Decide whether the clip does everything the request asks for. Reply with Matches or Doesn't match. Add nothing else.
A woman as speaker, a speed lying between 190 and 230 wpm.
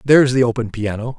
Doesn't match